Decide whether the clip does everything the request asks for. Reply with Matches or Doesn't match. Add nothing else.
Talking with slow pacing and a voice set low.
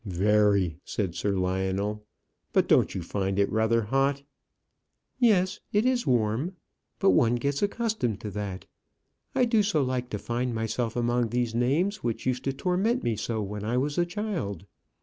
Doesn't match